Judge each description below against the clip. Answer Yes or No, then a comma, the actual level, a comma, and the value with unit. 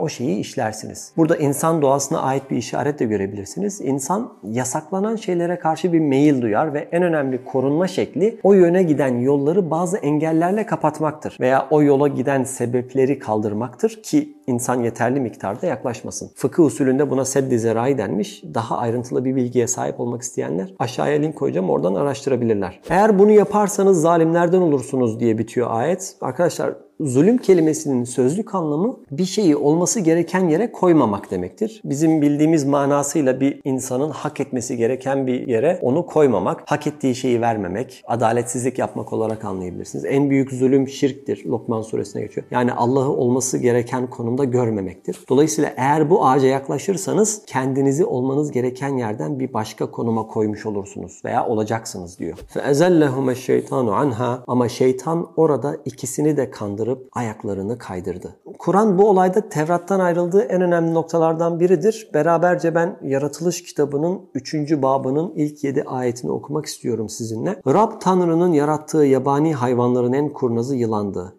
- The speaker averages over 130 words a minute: Yes, fast, 140 wpm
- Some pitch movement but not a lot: Yes, average, 5.0 semitones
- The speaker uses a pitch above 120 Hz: Yes, medium, 140 Hz